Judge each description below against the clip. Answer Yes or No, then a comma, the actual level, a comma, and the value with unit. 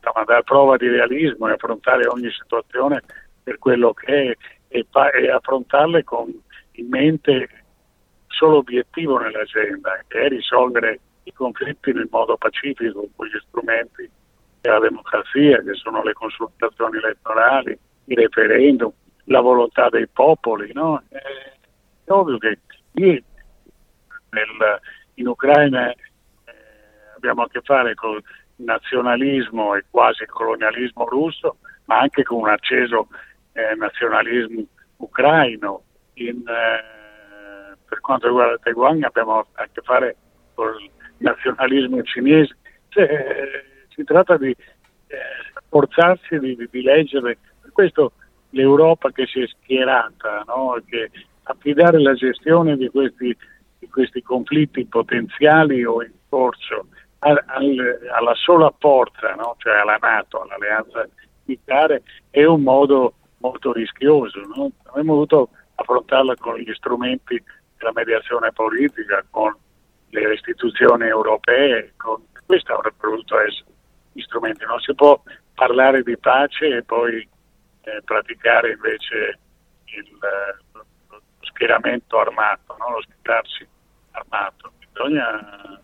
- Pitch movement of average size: Yes, average, 4.7 semitones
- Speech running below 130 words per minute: Yes, average, 120 wpm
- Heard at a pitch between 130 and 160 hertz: Yes, low, 135 Hz